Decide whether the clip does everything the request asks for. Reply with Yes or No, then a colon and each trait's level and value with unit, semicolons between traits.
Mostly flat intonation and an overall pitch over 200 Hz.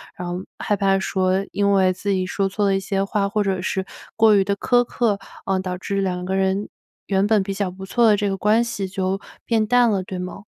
No: narrow, 1.5 semitones; high, 195 Hz